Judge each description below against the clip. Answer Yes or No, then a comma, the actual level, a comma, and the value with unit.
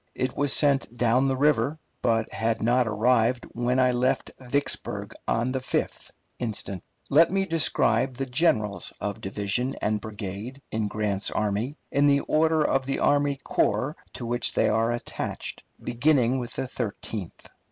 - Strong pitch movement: No, average, 3.7 semitones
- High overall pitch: No, low, 125 Hz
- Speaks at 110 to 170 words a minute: Yes, average, 155 wpm